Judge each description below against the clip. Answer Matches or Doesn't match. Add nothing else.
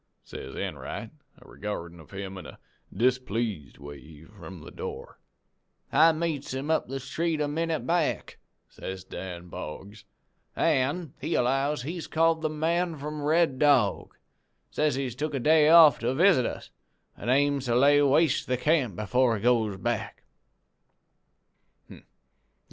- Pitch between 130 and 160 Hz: Matches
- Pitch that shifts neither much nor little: Doesn't match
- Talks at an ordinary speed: Matches